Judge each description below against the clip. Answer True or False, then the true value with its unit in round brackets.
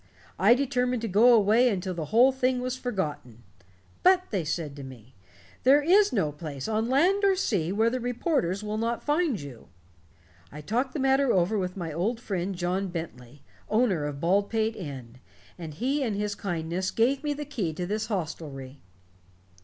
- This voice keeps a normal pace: True (175 wpm)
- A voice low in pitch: False (205 Hz)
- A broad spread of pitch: True (7.1 semitones)